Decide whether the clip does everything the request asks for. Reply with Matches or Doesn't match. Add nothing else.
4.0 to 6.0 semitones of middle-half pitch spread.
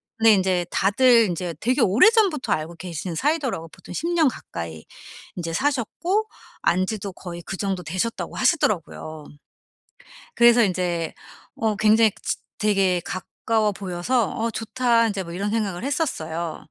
Matches